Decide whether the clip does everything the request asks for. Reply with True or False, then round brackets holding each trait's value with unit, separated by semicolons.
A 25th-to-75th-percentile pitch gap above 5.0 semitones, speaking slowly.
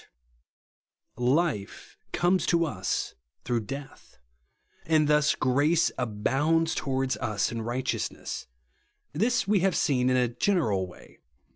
True (5.4 semitones; 120 wpm)